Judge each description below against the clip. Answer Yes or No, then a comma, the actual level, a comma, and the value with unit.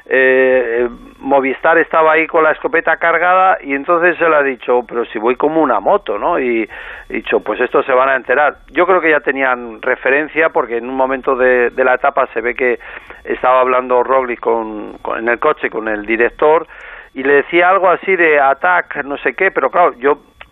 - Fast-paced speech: Yes, fast, 210 wpm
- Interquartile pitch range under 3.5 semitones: No, average, 4.8 semitones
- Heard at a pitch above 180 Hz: No, low, 135 Hz